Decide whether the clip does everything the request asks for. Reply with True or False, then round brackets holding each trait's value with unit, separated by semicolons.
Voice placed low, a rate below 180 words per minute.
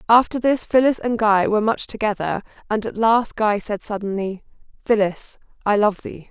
False (215 Hz; 170 wpm)